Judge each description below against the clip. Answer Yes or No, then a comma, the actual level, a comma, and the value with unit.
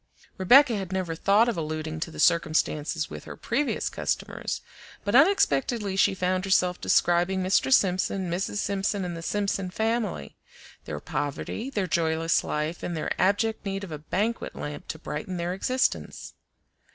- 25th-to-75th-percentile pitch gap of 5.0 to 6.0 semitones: No, average, 3.9 semitones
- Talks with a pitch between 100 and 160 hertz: No, medium, 185 Hz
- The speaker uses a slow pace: No, average, 155 wpm